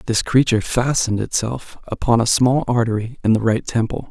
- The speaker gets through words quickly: No, average, 175 wpm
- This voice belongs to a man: Yes, male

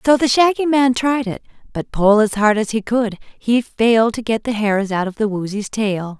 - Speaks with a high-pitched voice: Yes, high, 225 Hz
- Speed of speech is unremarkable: No, fast, 230 wpm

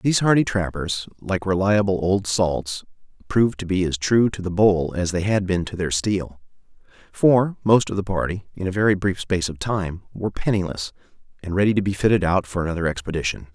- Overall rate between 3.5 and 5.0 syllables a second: No, 5.6 syllables/s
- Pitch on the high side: No, very low, 95 Hz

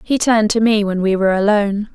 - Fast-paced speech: Yes, fast, 245 wpm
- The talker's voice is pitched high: Yes, high, 210 Hz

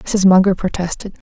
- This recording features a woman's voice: Yes, female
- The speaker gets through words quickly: No, average, 140 wpm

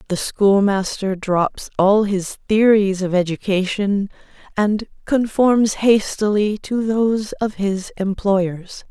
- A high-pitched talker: Yes, high, 200 Hz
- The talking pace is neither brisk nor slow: No, slow, 110 wpm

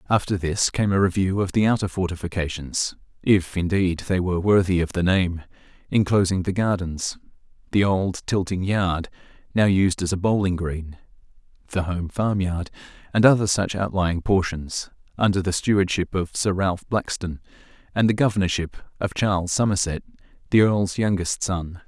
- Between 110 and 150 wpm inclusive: Yes, average, 145 wpm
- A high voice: No, very low, 95 Hz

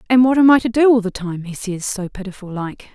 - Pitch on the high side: Yes, high, 210 Hz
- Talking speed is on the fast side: Yes, fast, 285 wpm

